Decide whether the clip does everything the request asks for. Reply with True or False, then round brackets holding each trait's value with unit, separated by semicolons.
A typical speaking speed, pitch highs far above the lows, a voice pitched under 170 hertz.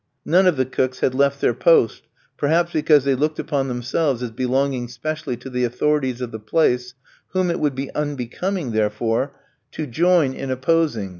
False (175 wpm; 3.9 semitones; 135 Hz)